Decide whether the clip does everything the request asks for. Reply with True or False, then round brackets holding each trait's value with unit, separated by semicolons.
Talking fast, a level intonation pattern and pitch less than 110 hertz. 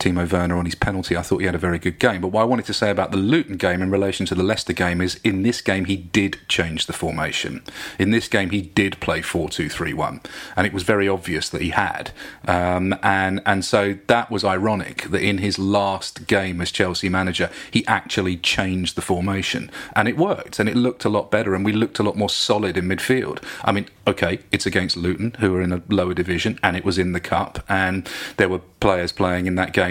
True (240 wpm; 2.0 semitones; 95 Hz)